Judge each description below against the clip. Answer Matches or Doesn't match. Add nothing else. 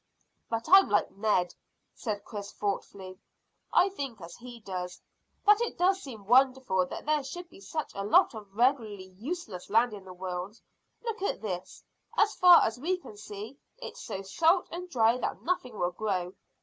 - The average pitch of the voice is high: Matches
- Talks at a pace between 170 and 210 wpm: Matches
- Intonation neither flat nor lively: Doesn't match